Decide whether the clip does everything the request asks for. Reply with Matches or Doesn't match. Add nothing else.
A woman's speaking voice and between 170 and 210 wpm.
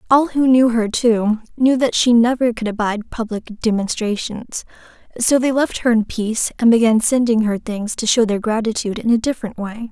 Matches